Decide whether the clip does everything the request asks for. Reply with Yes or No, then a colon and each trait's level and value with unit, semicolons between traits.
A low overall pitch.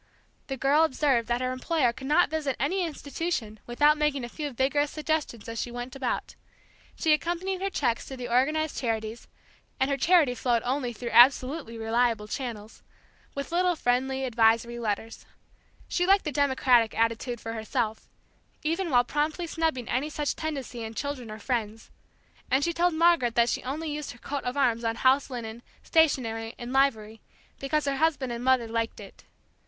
No: very high, 260 Hz